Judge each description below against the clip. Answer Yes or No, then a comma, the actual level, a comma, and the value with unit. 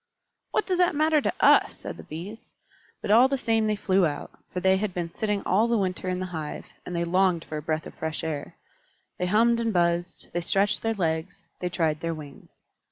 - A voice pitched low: No, medium, 185 Hz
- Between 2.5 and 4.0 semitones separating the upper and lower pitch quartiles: No, average, 4.5 semitones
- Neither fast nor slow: No, fast, 225 wpm